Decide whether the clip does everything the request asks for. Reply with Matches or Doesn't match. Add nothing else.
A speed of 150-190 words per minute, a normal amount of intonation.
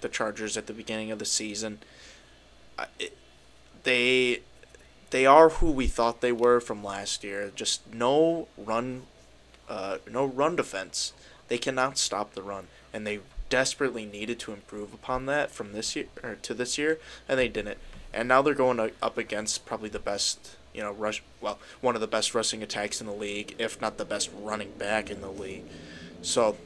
Matches